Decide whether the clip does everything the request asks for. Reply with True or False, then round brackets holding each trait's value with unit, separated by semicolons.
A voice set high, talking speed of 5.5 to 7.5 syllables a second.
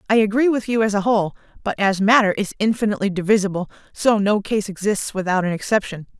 True (205 Hz; 6.5 syllables/s)